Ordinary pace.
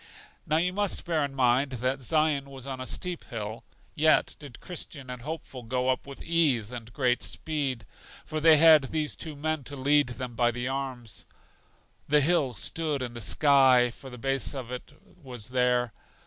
Yes: average, 185 wpm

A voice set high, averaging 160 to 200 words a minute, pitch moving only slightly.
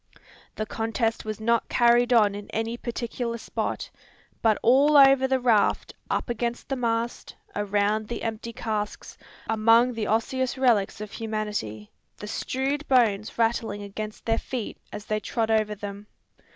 No: high, 225 Hz; average, 150 wpm; narrow, 2.2 semitones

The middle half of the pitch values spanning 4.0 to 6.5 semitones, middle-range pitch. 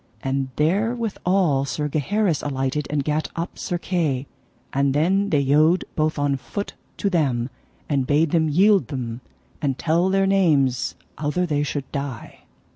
Yes: average, 4.5 semitones; medium, 150 Hz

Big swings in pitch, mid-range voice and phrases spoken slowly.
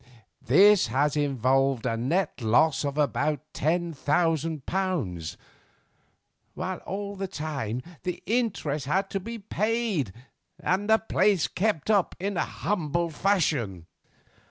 Yes: wide, 6.2 semitones; medium, 160 Hz; slow, 125 wpm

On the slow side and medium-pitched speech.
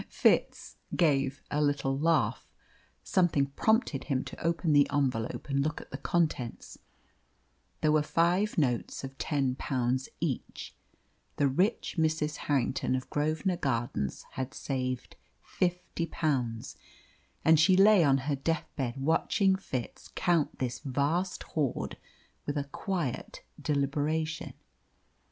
Yes: slow, 125 wpm; medium, 145 Hz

